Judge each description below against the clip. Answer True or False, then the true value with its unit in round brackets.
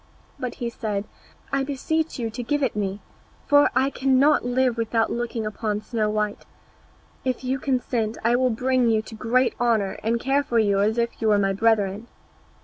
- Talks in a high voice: True (235 Hz)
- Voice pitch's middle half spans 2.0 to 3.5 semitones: True (3.1 semitones)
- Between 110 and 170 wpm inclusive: False (185 wpm)